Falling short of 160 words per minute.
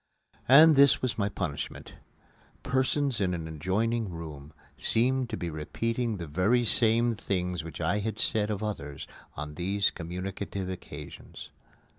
Yes: average, 140 wpm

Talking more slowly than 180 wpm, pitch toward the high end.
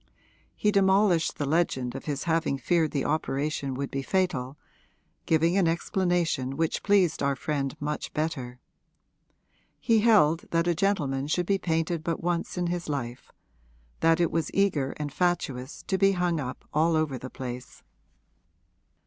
No: average, 155 wpm; medium, 160 Hz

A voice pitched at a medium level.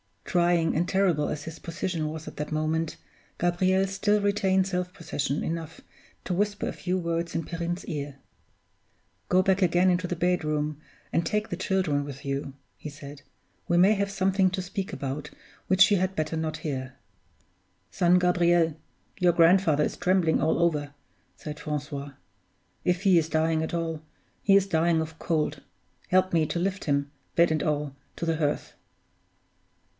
Yes: medium, 170 Hz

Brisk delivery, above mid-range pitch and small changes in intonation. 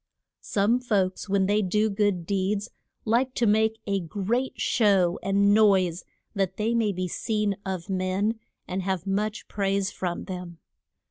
No: average, 150 wpm; high, 200 Hz; narrow, 2.3 semitones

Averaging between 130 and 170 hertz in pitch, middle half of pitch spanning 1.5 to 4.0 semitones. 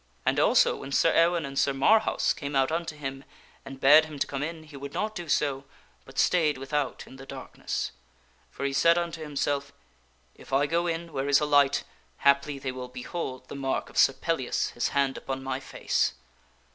Yes: medium, 140 Hz; average, 2.8 semitones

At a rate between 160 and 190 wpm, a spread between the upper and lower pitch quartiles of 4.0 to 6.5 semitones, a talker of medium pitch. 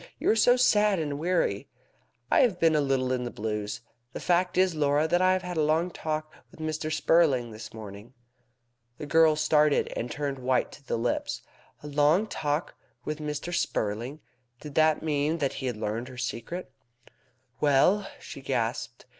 Yes: average, 180 wpm; average, 4.4 semitones; medium, 150 Hz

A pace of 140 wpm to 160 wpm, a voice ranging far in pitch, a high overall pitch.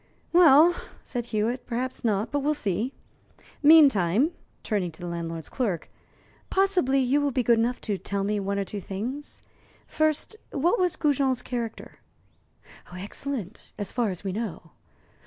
Yes: average, 150 wpm; wide, 6.0 semitones; high, 240 Hz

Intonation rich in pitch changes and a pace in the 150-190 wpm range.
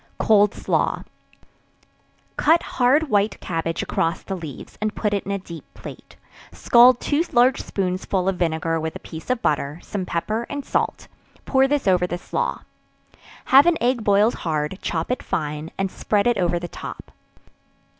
Yes: wide, 6.3 semitones; average, 165 wpm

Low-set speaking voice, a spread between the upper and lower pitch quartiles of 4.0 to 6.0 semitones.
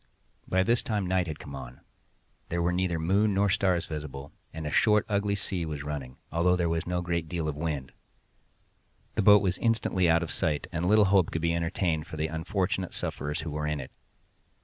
No: very low, 85 Hz; average, 3.4 semitones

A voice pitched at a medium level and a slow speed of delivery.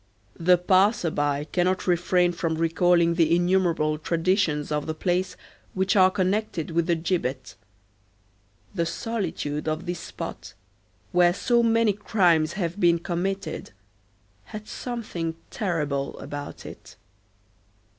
Yes: medium, 175 Hz; slow, 120 wpm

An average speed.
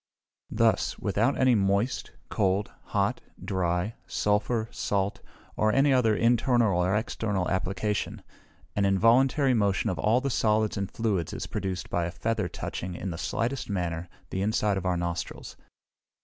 Yes: average, 150 wpm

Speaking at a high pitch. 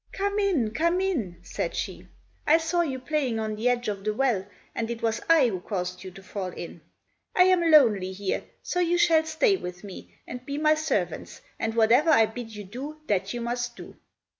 Yes: high, 245 Hz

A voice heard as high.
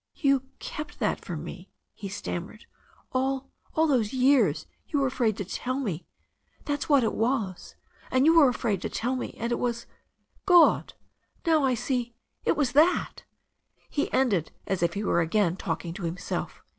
Yes: high, 245 Hz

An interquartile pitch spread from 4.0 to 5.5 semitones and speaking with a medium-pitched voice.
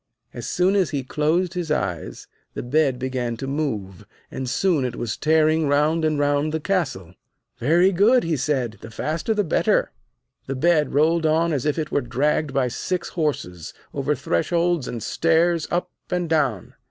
Yes: average, 4.4 semitones; medium, 150 Hz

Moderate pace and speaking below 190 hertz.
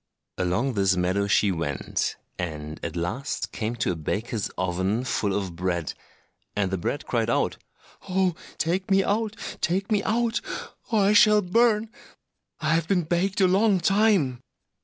Yes: average, 160 wpm; low, 135 Hz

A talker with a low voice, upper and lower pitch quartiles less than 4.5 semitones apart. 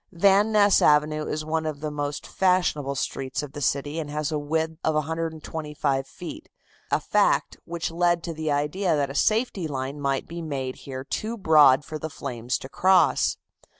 No: medium, 155 Hz; average, 2.9 semitones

